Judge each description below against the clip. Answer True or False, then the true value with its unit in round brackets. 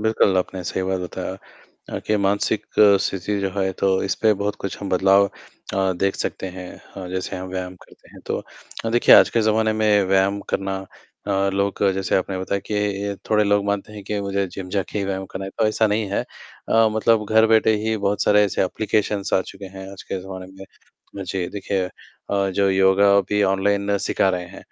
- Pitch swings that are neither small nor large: False (1.4 semitones)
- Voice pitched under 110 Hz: True (100 Hz)